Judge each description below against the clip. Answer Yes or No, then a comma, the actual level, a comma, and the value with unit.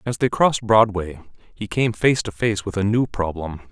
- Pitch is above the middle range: No, low, 105 Hz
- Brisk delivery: Yes, fast, 210 wpm